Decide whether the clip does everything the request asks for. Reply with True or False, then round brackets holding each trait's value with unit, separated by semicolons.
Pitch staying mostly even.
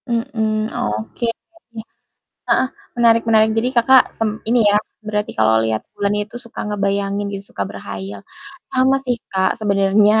False (3.0 semitones)